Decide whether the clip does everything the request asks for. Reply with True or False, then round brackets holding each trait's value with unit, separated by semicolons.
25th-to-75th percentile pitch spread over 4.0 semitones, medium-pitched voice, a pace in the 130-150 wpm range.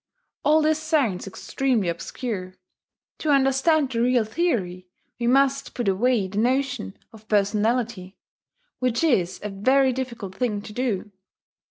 False (4.9 semitones; 235 Hz; 135 wpm)